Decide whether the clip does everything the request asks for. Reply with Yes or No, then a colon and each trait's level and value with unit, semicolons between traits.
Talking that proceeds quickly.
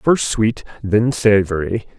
No: slow, 120 wpm